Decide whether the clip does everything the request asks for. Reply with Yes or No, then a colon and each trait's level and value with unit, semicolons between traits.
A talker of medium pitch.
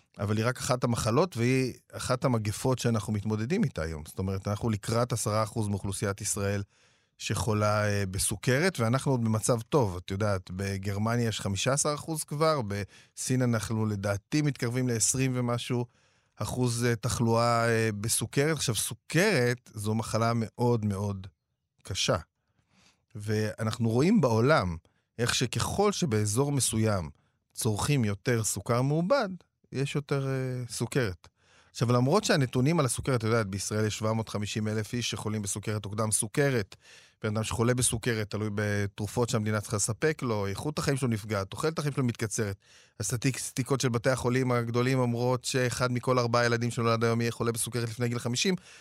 No: low, 115 Hz